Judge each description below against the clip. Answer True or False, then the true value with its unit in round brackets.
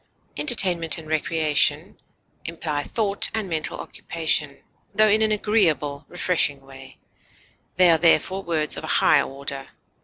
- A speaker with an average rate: False (130 wpm)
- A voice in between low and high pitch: True (165 Hz)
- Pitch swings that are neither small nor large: True (4.6 semitones)